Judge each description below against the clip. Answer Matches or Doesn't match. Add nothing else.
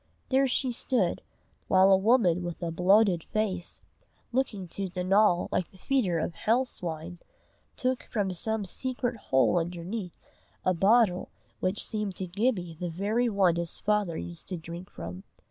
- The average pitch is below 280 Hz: Matches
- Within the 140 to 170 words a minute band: Matches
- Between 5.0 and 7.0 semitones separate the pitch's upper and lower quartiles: Doesn't match